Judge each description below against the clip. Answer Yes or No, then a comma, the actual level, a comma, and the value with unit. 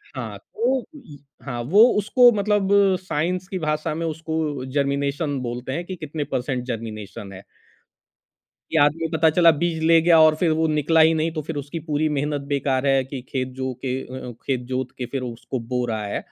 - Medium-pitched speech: Yes, medium, 145 Hz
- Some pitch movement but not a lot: Yes, average, 3.9 semitones